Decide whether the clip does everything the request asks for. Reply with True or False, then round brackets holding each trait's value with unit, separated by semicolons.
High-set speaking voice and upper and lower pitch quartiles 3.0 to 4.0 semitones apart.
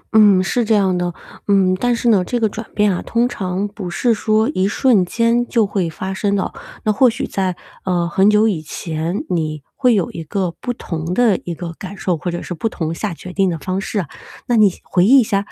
True (195 Hz; 3.6 semitones)